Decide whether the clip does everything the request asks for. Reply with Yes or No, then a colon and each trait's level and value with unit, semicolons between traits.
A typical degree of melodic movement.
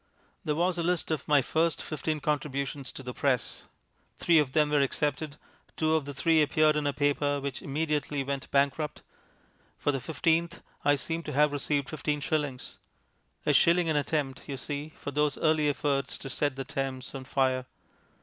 No: narrow, 2.1 semitones